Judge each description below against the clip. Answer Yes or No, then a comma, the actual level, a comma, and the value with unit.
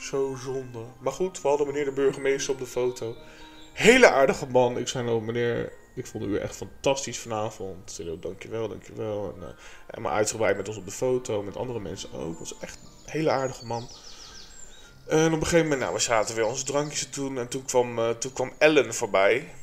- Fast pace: Yes, fast, 215 wpm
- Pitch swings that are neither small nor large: Yes, average, 3.2 semitones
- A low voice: Yes, low, 130 Hz